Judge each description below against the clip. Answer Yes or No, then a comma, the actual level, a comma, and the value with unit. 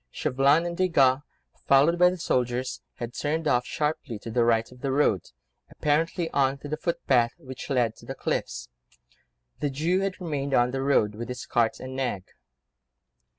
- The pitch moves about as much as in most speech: Yes, average, 3.9 semitones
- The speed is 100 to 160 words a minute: No, average, 175 wpm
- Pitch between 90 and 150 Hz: Yes, low, 135 Hz